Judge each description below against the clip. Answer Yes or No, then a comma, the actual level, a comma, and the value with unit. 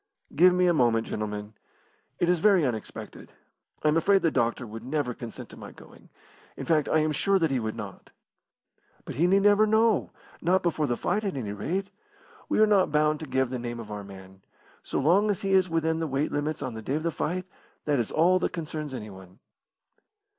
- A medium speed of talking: No, fast, 215 wpm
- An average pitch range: No, wide, 7.2 semitones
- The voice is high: No, medium, 155 Hz